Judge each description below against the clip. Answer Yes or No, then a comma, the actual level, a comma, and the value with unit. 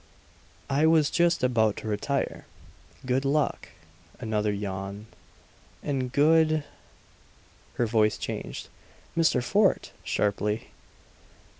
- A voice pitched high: No, low, 125 Hz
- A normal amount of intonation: No, wide, 6.3 semitones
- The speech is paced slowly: Yes, slow, 100 wpm